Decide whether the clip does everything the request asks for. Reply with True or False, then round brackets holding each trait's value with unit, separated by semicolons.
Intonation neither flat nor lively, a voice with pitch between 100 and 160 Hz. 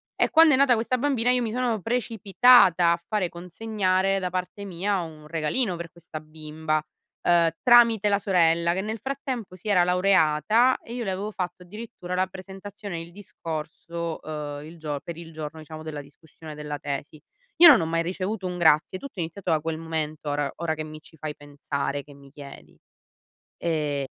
False (4.7 semitones; 175 Hz)